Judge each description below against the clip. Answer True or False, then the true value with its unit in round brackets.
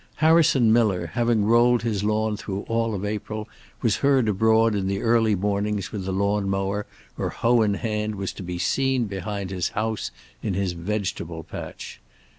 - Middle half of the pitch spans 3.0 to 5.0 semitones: False (2.5 semitones)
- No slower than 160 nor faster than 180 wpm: True (175 wpm)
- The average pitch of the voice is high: False (105 Hz)